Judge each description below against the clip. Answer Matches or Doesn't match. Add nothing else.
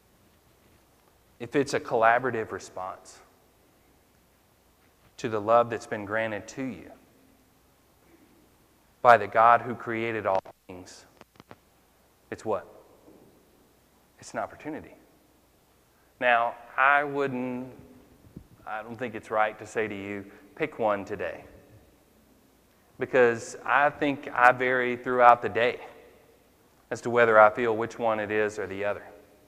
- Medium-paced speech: Doesn't match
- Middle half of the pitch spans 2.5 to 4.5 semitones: Matches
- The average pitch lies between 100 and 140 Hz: Matches